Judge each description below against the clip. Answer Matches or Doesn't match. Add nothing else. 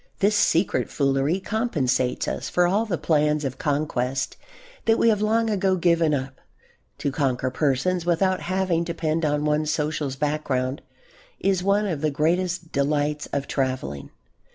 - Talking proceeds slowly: Doesn't match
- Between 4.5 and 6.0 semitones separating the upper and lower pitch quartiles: Matches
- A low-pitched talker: Doesn't match